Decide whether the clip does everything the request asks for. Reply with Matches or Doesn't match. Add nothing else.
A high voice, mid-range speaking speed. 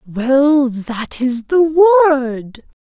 Doesn't match